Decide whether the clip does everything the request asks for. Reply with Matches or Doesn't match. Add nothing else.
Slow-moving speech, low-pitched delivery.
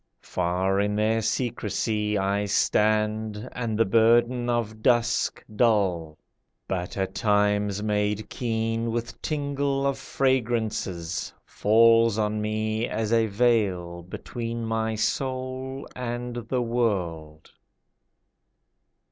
Matches